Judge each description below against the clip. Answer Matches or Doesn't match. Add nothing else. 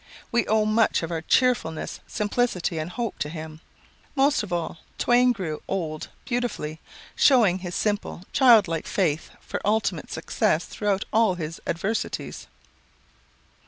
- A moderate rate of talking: Doesn't match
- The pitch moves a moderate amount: Doesn't match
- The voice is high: Matches